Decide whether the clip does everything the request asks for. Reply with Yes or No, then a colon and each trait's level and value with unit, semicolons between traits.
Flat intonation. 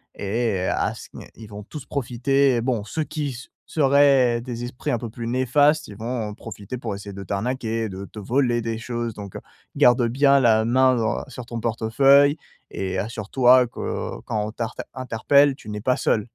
No: average, 3.0 semitones